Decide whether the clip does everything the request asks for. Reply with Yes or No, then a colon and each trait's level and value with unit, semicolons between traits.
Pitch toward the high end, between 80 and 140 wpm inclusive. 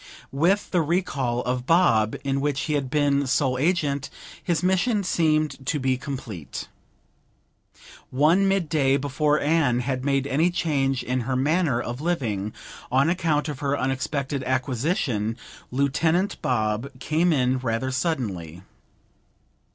No: medium, 140 Hz; slow, 135 wpm